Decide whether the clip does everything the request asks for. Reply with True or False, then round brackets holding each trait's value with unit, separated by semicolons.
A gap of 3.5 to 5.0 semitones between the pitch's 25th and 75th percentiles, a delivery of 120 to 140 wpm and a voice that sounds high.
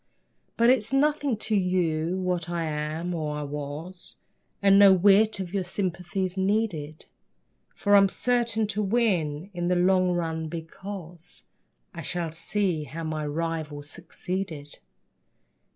False (3.8 semitones; 135 wpm; 180 Hz)